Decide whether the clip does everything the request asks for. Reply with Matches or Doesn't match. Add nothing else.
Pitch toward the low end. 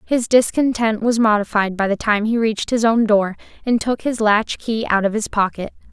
Doesn't match